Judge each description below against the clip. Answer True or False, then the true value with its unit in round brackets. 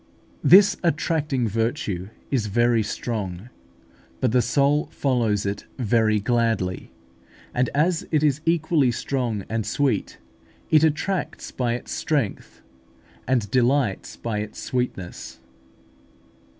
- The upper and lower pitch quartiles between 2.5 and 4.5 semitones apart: False (5.1 semitones)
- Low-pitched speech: True (120 Hz)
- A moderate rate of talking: False (110 wpm)